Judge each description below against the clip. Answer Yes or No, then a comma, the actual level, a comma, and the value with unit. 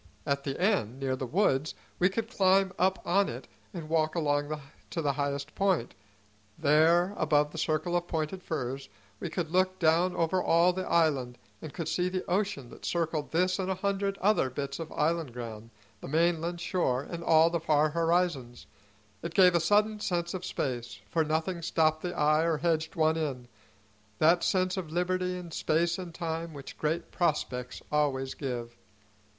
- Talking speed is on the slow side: No, average, 180 wpm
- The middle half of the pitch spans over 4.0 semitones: No, average, 3.5 semitones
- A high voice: No, medium, 165 Hz